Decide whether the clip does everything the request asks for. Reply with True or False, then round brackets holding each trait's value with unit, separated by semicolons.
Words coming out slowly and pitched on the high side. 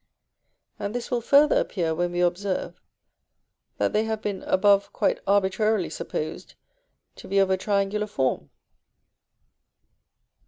True (125 wpm; 200 Hz)